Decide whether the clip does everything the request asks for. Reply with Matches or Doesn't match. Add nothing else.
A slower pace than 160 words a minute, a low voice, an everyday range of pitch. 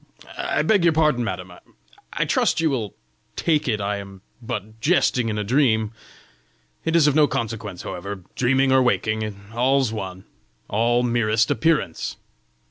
Matches